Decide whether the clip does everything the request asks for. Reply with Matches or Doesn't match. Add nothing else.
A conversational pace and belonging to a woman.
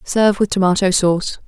Matches